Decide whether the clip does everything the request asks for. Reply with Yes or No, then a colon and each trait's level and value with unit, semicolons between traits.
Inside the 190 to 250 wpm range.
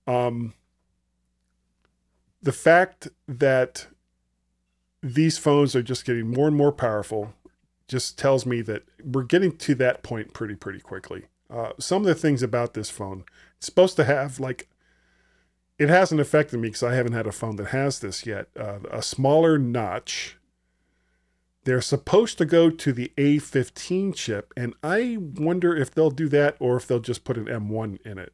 No: average, 170 wpm